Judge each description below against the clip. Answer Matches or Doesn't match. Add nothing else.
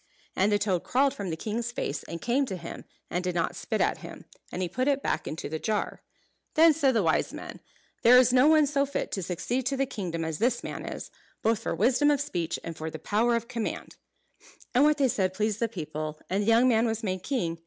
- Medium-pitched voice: Doesn't match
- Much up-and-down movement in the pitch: Matches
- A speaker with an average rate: Doesn't match